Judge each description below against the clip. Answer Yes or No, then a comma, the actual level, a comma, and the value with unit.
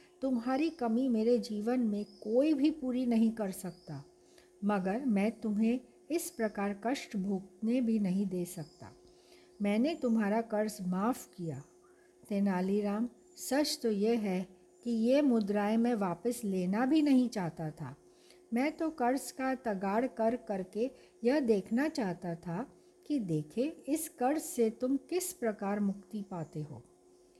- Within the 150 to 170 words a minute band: No, average, 140 wpm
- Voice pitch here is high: Yes, high, 225 Hz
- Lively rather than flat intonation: No, average, 5.0 semitones